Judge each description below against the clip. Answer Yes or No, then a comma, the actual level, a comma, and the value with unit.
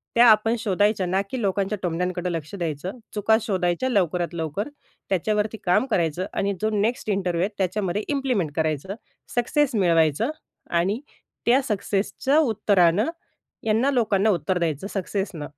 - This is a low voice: No, high, 195 Hz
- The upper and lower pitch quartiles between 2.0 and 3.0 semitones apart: No, average, 3.8 semitones